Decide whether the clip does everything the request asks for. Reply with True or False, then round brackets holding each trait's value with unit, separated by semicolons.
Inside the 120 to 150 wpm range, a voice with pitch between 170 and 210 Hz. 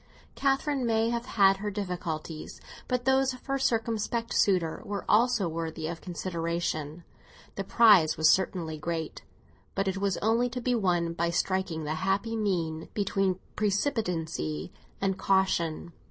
True (140 wpm; 190 Hz)